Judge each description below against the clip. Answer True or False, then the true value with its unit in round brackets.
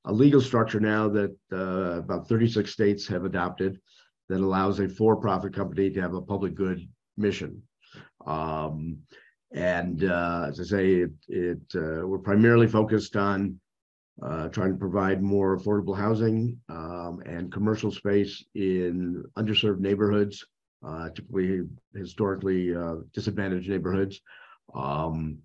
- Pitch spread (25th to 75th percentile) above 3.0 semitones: False (2.7 semitones)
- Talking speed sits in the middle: False (130 wpm)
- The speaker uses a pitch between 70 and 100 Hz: True (95 Hz)